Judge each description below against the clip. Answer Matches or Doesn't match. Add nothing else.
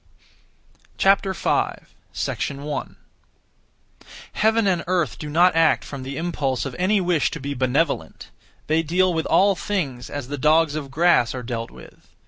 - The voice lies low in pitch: Doesn't match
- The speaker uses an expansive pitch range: Doesn't match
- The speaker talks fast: Doesn't match